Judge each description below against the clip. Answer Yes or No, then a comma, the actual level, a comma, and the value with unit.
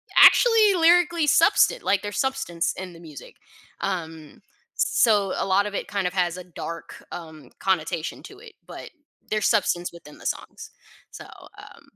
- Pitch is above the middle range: Yes, high, 195 Hz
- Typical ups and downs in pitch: No, wide, 8.6 semitones